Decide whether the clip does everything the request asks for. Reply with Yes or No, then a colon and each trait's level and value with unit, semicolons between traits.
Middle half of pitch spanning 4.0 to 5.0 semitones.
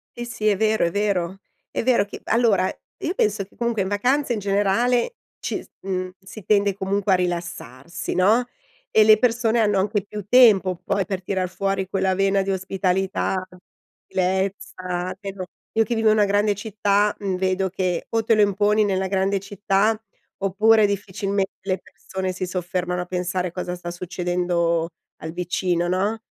No: narrow, 2.4 semitones